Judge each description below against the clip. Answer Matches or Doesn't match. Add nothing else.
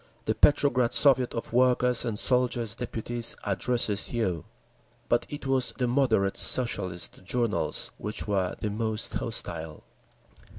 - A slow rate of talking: Matches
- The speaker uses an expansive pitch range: Doesn't match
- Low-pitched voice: Matches